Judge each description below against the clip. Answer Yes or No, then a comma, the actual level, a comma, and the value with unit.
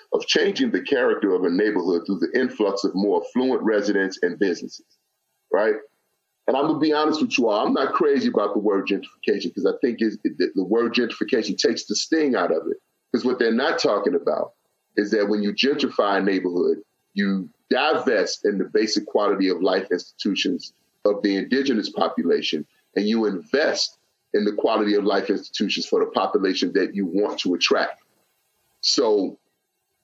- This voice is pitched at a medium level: No, low, 115 Hz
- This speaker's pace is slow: No, average, 180 wpm